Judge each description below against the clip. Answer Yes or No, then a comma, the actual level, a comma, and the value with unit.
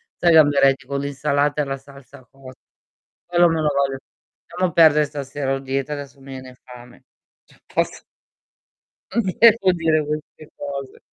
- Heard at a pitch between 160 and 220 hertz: No, medium, 140 Hz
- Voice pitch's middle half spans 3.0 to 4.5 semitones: No, narrow, 2.4 semitones